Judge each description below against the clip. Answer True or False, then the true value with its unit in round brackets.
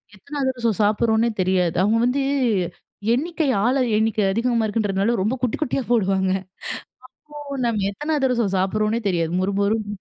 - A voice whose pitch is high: True (220 Hz)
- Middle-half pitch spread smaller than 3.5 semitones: False (3.8 semitones)